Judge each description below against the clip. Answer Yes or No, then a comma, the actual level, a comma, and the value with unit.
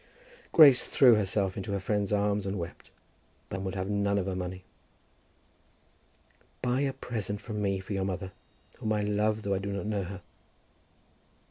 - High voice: No, low, 100 Hz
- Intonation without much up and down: Yes, narrow, 1.7 semitones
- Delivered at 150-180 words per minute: Yes, average, 170 wpm